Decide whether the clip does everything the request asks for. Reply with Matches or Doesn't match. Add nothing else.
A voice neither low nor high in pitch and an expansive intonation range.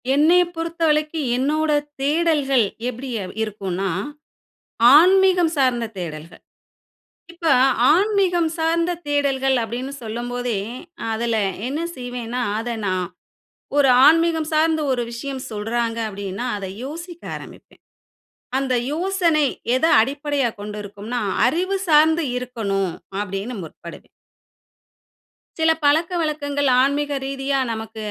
Doesn't match